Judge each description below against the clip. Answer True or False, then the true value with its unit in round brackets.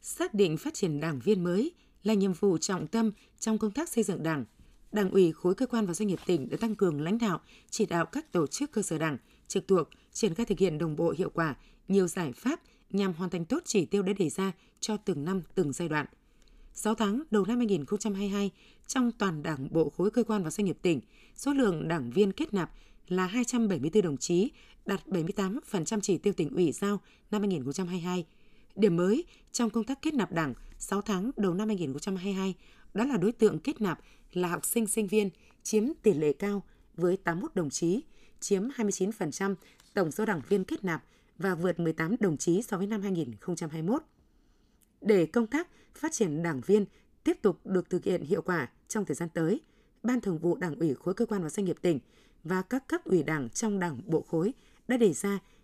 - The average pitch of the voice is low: False (195 Hz)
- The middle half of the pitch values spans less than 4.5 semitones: True (3.9 semitones)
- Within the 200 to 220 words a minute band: True (210 wpm)